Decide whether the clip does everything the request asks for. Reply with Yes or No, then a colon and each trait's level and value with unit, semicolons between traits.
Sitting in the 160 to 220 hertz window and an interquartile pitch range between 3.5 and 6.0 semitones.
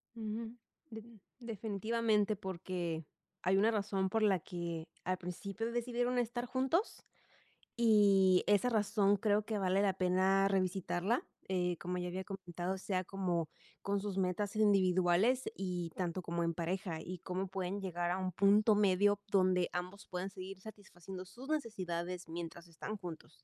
No: high, 190 Hz; average, 2.8 semitones